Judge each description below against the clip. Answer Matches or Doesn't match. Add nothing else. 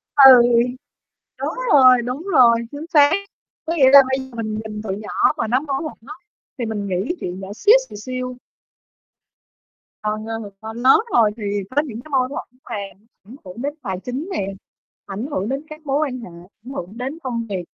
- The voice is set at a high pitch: Matches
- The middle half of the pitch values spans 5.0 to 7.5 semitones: Doesn't match